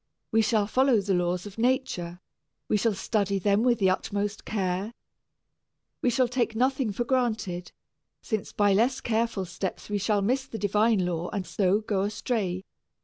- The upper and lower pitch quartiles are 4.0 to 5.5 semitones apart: No, average, 3.5 semitones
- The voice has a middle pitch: No, high, 210 Hz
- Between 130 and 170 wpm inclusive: Yes, average, 165 wpm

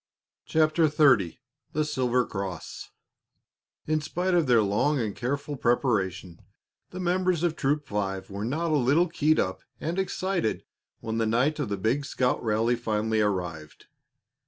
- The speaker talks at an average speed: Yes, average, 150 wpm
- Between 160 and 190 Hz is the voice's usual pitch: No, low, 125 Hz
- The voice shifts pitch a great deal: Yes, wide, 6.7 semitones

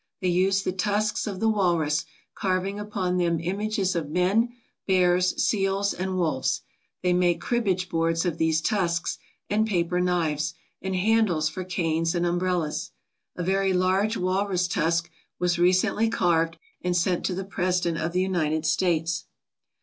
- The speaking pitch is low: No, medium, 180 Hz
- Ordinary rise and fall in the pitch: No, narrow, 2.3 semitones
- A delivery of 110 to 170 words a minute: Yes, average, 150 wpm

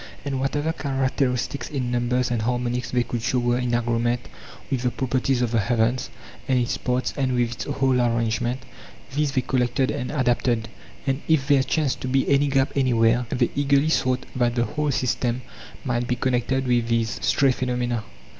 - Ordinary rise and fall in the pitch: No, narrow, 1.9 semitones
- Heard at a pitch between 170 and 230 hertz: No, low, 125 Hz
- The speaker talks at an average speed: Yes, average, 185 wpm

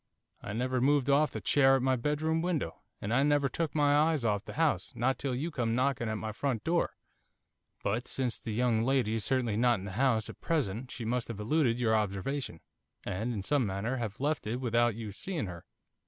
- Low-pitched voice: Yes, low, 125 Hz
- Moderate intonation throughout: Yes, average, 4.4 semitones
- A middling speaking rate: No, fast, 215 wpm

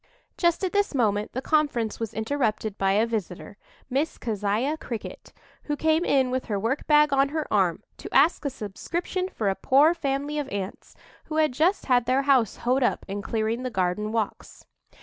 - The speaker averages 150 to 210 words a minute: Yes, average, 190 wpm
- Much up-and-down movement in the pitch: Yes, wide, 5.7 semitones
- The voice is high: Yes, very high, 255 Hz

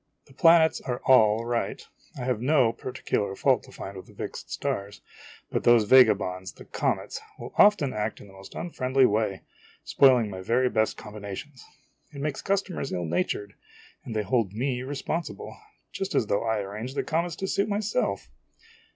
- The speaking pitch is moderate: No, low, 120 Hz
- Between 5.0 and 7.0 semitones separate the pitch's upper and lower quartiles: Yes, wide, 5.4 semitones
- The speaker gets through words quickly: No, average, 170 wpm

